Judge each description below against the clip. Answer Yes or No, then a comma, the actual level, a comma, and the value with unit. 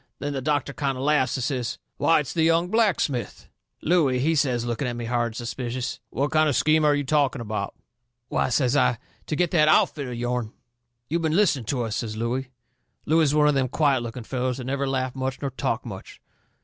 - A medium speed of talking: No, fast, 225 wpm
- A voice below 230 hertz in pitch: Yes, low, 135 Hz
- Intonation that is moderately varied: Yes, average, 3.6 semitones